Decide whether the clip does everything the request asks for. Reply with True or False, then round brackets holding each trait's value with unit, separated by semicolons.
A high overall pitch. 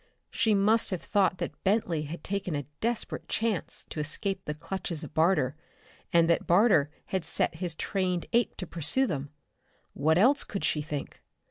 False (180 Hz)